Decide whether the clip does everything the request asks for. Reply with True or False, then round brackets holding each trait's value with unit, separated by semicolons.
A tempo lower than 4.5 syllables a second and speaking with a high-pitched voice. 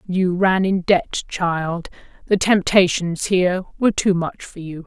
False (4.1 syllables/s; 180 Hz)